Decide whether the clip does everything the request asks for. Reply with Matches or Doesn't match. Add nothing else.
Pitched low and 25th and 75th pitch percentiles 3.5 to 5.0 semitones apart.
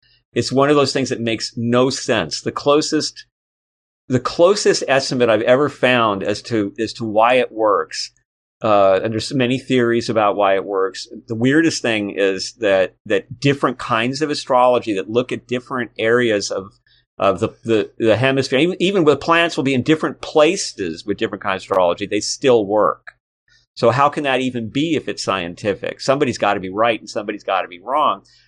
Matches